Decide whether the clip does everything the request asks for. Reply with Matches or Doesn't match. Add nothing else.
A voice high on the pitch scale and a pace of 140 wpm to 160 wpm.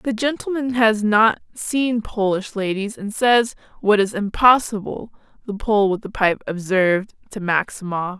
Matches